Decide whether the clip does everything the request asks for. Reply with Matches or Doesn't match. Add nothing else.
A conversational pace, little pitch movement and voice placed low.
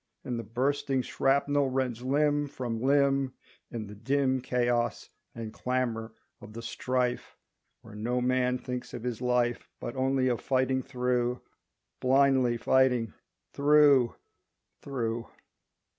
Doesn't match